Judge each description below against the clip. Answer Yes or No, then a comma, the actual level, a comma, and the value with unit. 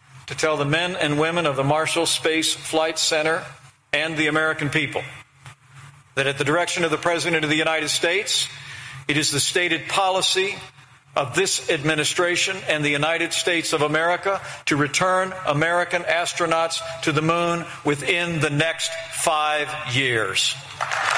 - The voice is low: No, medium, 155 Hz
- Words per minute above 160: No, average, 150 wpm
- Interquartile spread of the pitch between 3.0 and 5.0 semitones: No, narrow, 2.5 semitones